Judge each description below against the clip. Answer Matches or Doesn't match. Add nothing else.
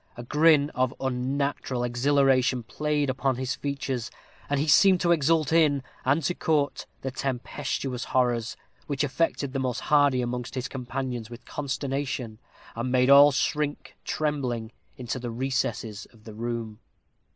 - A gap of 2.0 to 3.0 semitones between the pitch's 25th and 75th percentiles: Matches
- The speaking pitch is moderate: Doesn't match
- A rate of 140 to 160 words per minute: Matches